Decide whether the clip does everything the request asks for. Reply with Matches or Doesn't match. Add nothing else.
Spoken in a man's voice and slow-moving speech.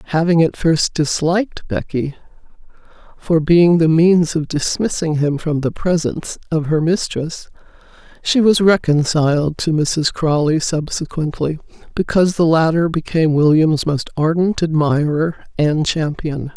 Doesn't match